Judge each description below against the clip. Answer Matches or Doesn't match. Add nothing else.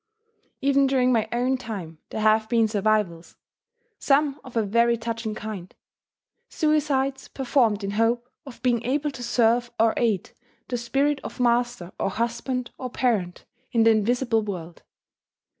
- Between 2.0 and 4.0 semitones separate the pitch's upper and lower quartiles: Matches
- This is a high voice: Matches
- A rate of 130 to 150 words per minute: Matches